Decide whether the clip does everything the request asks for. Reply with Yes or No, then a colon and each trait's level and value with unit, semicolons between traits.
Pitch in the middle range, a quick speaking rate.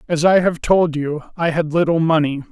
Yes: medium, 160 Hz; fast, 215 wpm